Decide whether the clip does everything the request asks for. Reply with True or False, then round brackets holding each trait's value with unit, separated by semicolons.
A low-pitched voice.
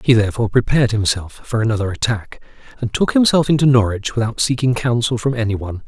True (115 Hz)